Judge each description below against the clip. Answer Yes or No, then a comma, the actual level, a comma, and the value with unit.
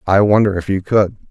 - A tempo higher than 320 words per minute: No, fast, 230 wpm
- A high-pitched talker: No, low, 100 Hz